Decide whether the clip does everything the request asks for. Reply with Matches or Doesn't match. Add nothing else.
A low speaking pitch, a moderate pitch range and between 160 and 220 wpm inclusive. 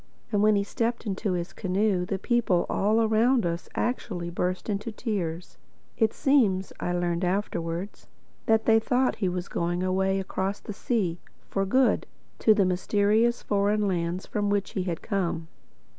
Doesn't match